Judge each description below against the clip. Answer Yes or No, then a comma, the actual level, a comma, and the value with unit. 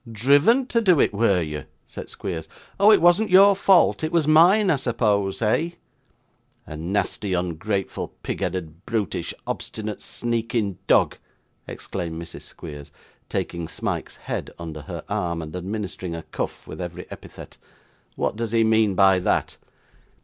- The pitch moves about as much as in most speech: No, wide, 9.0 semitones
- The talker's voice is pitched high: No, low, 105 Hz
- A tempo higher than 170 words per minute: No, average, 150 wpm